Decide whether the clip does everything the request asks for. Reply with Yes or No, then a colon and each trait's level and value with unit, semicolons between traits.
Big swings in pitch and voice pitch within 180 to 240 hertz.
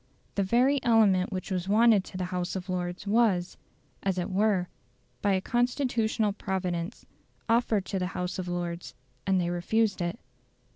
No: average, 3.4 semitones; high, 190 Hz